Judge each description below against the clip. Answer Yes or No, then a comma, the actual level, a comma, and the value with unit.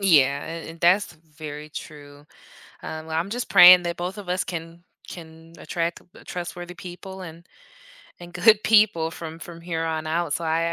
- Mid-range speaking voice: Yes, medium, 170 Hz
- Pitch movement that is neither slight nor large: No, narrow, 1.8 semitones